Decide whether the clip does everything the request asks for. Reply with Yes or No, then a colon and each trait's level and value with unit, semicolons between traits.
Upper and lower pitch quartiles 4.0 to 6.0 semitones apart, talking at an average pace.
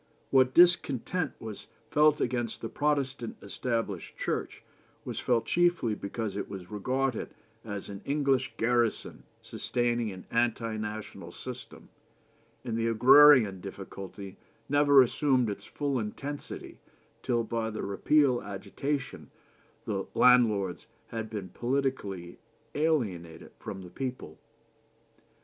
No: average, 4.8 semitones; slow, 115 wpm